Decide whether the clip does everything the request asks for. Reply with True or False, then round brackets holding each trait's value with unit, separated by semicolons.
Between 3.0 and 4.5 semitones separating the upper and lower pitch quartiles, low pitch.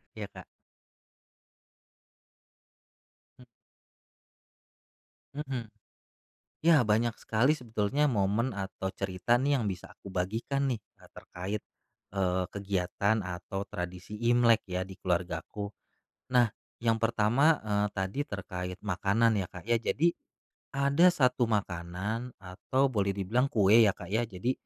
True (4.2 semitones; 105 Hz)